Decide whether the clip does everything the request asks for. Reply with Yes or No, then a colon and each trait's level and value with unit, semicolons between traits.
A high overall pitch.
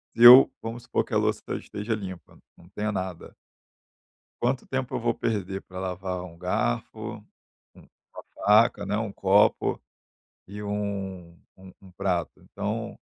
No: low, 100 Hz